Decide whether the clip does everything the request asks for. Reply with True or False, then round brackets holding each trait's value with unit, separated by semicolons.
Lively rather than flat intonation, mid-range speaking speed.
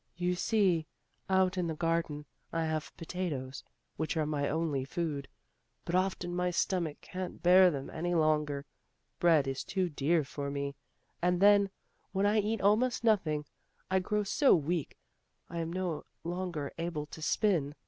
False (3.6 semitones; 160 wpm)